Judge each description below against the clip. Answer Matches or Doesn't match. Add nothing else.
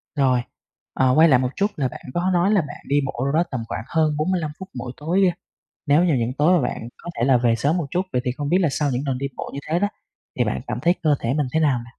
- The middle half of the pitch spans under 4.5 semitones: Doesn't match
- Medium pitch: Matches